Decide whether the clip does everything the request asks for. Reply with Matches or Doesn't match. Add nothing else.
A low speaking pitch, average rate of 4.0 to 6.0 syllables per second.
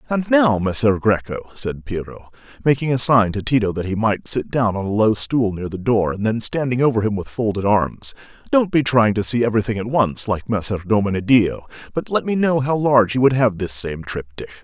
Matches